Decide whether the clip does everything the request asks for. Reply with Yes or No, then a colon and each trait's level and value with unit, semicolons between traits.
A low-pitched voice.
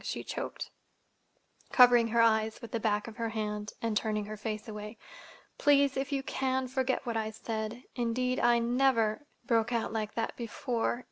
No: high, 230 Hz